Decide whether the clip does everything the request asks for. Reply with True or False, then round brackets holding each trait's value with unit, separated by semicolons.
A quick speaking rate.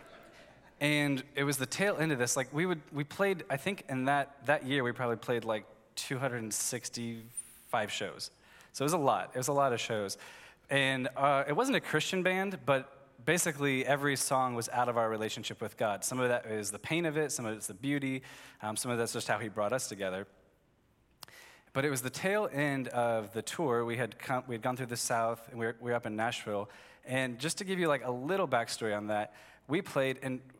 True (230 wpm)